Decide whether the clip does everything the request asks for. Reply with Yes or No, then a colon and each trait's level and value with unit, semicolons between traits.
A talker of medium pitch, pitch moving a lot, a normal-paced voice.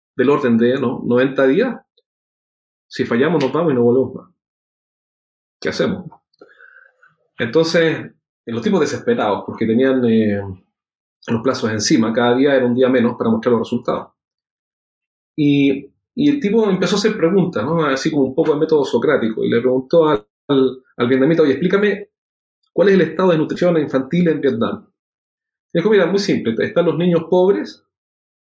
Yes: medium, 145 Hz; wide, 5.7 semitones; average, 170 wpm